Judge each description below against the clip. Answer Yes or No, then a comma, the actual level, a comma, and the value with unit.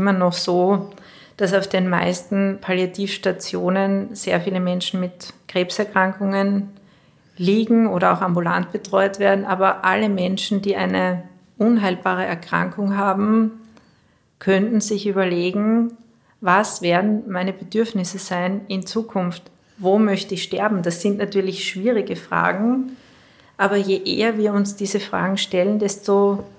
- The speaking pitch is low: No, high, 195 Hz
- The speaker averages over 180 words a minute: No, slow, 125 wpm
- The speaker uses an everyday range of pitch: No, narrow, 1.8 semitones